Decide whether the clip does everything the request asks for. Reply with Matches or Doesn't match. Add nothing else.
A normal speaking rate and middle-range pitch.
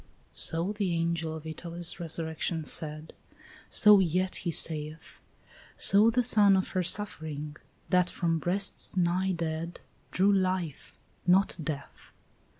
Doesn't match